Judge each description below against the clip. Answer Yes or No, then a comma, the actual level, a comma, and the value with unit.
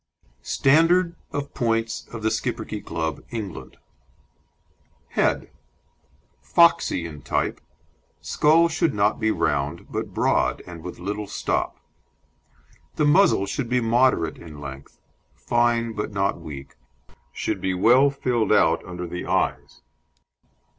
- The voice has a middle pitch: No, low, 110 Hz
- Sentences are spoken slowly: Yes, slow, 120 wpm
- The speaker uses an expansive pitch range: Yes, wide, 7.4 semitones